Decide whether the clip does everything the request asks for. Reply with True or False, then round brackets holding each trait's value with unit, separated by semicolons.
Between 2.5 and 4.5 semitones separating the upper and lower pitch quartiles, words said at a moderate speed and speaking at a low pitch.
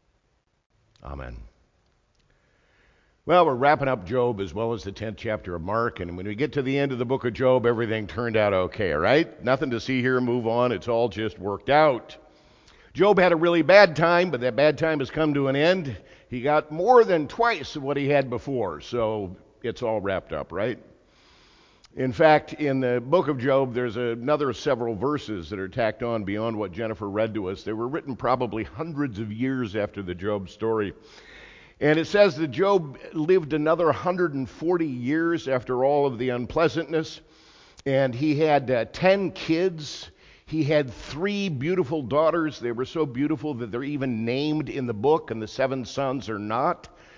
False (5.4 semitones; 185 wpm; 130 Hz)